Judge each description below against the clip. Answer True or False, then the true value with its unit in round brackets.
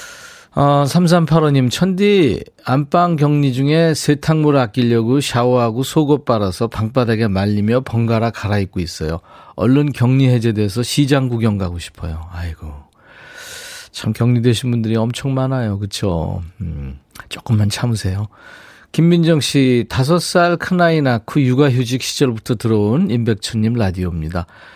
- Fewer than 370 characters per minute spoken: True (285 characters per minute)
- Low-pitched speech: True (120 Hz)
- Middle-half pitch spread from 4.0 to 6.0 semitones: True (5.5 semitones)